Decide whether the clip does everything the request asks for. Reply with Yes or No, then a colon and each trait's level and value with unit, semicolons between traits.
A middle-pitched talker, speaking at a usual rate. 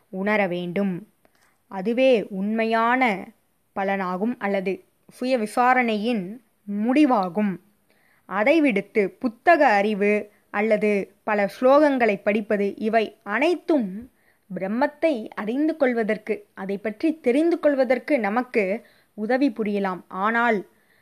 No: high, 215 Hz; average, 85 wpm